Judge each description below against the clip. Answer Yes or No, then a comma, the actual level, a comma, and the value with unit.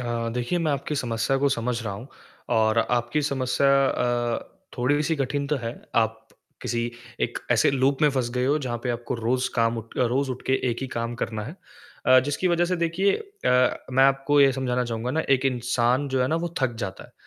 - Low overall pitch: Yes, low, 125 Hz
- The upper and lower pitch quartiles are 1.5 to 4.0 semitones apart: Yes, average, 2.9 semitones